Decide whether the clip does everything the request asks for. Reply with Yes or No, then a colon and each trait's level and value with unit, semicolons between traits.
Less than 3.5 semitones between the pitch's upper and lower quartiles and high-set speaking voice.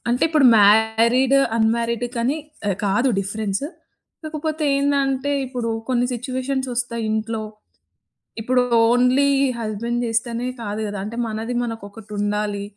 Yes: average, 2.9 semitones; high, 235 Hz